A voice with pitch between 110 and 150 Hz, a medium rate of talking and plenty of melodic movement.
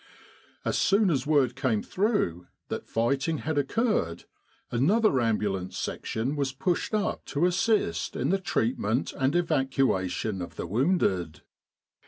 No: low, 135 Hz; slow, 130 wpm; wide, 8.7 semitones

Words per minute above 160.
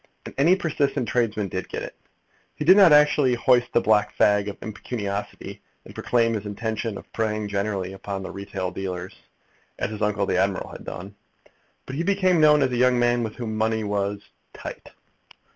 Yes: average, 185 wpm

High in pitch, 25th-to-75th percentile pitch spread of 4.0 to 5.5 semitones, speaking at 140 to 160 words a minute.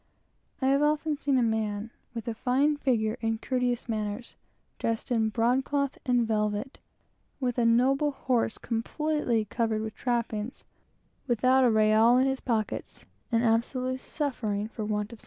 No: high, 235 Hz; average, 3.0 semitones; average, 155 wpm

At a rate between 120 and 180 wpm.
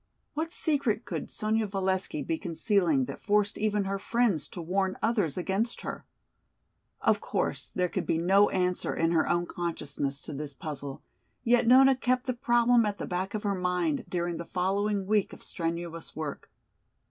Yes: average, 170 wpm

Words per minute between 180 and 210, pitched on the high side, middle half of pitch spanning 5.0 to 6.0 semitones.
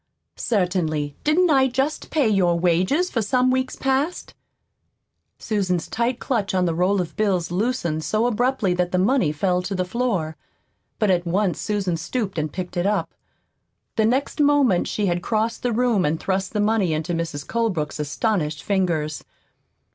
No: average, 170 wpm; high, 195 Hz; wide, 5.5 semitones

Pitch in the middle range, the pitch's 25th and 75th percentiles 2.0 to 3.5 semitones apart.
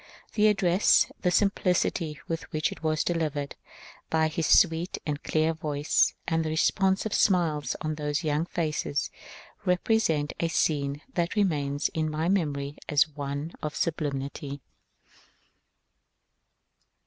Yes: medium, 155 Hz; average, 2.8 semitones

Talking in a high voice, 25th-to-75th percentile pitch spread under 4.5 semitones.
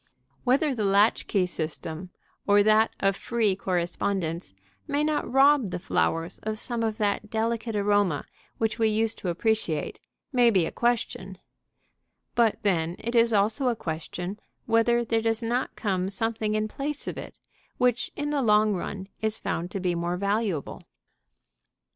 Yes: high, 215 Hz; average, 3.6 semitones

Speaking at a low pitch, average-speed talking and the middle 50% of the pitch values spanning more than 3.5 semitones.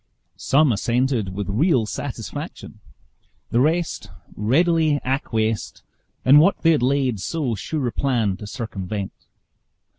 No: low, 125 Hz; slow, 120 wpm; wide, 5.4 semitones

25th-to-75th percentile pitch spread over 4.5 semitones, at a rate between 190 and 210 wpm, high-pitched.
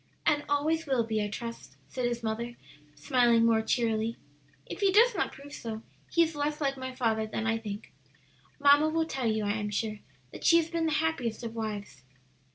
Yes: average, 5.1 semitones; average, 200 wpm; high, 240 Hz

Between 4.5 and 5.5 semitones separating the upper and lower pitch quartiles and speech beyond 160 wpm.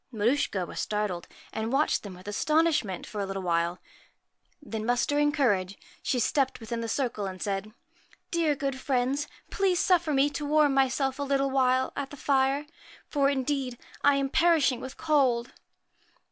Yes: average, 4.8 semitones; average, 170 wpm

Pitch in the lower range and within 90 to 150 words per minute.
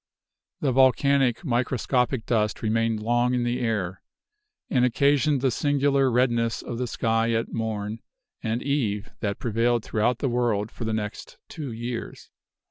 Yes: low, 120 Hz; average, 145 wpm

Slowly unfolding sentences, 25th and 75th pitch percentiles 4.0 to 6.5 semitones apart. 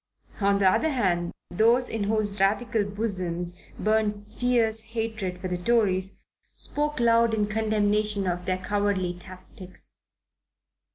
No: slow, 125 wpm; average, 3.1 semitones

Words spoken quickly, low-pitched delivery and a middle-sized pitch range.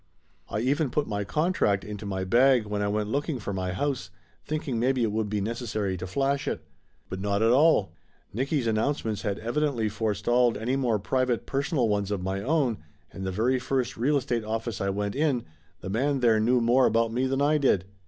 Yes: fast, 210 wpm; low, 115 Hz; average, 4.5 semitones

